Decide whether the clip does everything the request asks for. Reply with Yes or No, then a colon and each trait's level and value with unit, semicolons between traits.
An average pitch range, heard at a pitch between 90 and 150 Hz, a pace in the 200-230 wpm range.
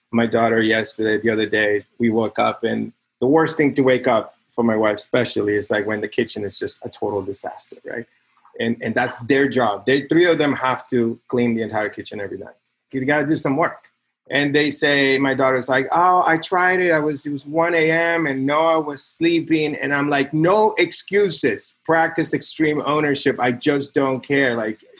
Yes: average, 4.7 semitones; medium, 140 Hz; fast, 205 wpm